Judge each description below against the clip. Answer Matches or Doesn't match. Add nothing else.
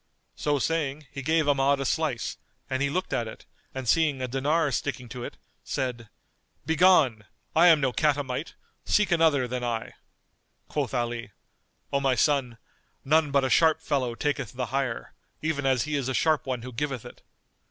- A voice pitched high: Doesn't match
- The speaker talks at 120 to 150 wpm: Doesn't match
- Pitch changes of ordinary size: Matches